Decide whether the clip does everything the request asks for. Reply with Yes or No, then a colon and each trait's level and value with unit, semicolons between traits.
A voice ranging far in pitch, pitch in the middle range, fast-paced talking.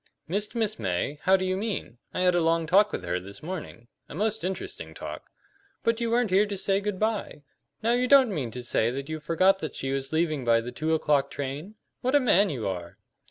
Yes: wide, 7.2 semitones; medium, 175 Hz; fast, 230 wpm